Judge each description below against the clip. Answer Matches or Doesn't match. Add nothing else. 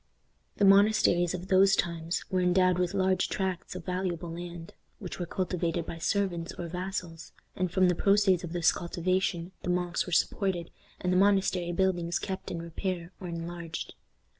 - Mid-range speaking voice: Matches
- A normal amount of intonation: Doesn't match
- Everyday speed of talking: Matches